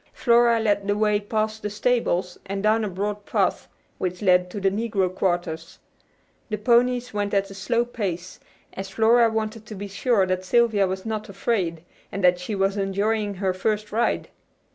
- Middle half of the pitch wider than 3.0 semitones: No, average, 2.7 semitones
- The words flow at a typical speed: Yes, average, 180 wpm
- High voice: Yes, high, 205 Hz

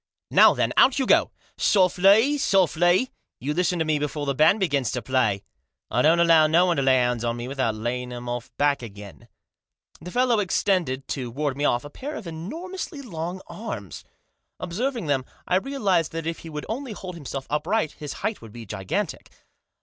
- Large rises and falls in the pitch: Yes, wide, 7.0 semitones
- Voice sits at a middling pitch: Yes, medium, 160 Hz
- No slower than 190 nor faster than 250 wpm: Yes, average, 195 wpm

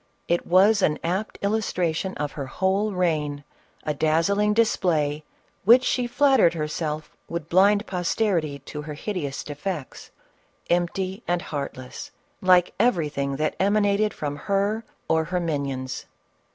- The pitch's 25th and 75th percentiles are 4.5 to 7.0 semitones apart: Yes, average, 5.0 semitones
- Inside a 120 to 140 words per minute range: Yes, slow, 135 wpm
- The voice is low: No, medium, 175 Hz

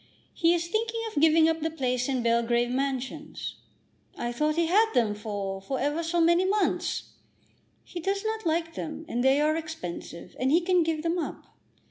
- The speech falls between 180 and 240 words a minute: Yes, average, 185 wpm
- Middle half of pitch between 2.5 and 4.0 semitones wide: No, average, 5.2 semitones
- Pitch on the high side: Yes, very high, 315 Hz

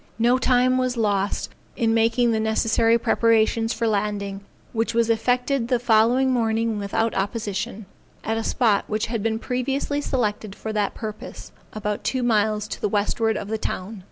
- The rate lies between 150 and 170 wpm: Yes, average, 165 wpm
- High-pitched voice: Yes, high, 225 Hz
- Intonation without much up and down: Yes, narrow, 2.1 semitones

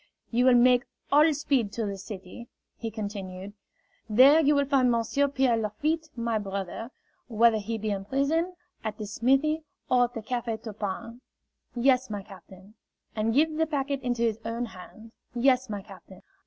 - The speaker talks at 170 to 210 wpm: Yes, average, 175 wpm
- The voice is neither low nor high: No, high, 235 Hz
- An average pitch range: Yes, average, 4.2 semitones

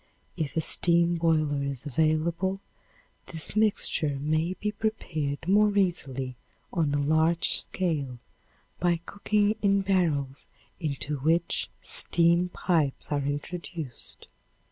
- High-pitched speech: No, medium, 165 Hz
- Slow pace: Yes, slow, 110 wpm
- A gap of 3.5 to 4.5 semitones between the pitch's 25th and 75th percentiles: Yes, average, 3.9 semitones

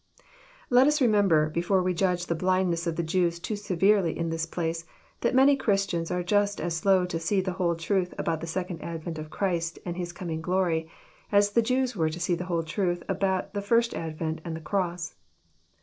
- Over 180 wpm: Yes, fast, 205 wpm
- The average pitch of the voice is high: No, medium, 180 Hz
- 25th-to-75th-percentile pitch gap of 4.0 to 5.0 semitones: No, average, 3.1 semitones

